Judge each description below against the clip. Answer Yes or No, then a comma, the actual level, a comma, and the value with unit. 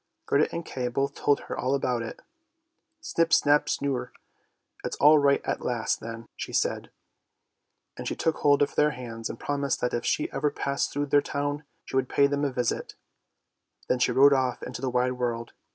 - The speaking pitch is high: No, medium, 140 Hz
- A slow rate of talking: No, average, 200 wpm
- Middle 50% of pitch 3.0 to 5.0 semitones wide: No, narrow, 2.6 semitones